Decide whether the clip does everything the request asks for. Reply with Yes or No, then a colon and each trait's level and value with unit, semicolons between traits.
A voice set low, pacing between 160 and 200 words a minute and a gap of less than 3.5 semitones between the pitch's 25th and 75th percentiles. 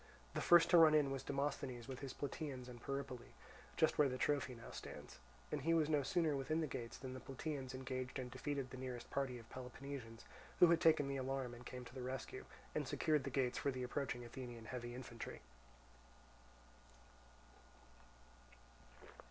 Yes: low, 130 Hz; average, 175 wpm; narrow, 2.4 semitones